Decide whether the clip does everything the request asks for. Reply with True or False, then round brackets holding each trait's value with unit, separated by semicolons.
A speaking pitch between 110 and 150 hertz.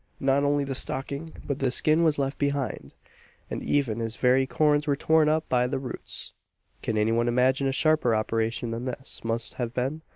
True (135 Hz)